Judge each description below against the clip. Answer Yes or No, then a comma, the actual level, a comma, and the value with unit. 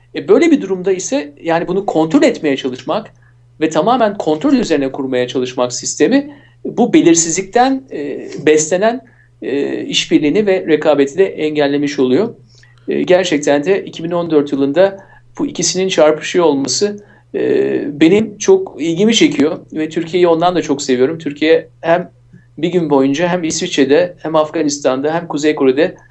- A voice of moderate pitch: Yes, medium, 165 Hz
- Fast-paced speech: No, average, 125 wpm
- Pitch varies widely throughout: Yes, wide, 5.7 semitones